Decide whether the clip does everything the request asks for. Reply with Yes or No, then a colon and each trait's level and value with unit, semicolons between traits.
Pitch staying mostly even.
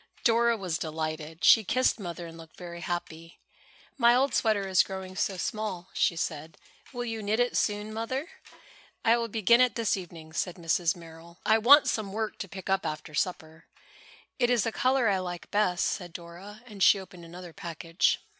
No: average, 4.7 semitones